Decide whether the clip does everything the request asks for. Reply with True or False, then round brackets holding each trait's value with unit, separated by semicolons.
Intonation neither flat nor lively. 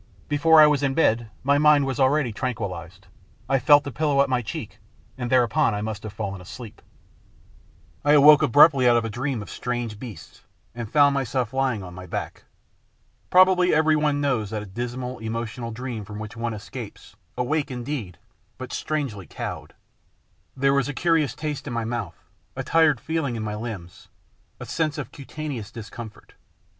True (4.7 semitones)